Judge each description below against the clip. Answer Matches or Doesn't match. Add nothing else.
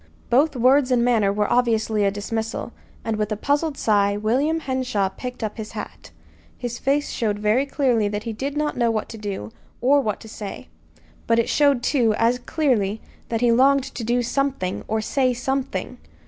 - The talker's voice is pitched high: Matches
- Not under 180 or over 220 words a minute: Matches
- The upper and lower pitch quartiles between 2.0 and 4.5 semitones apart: Matches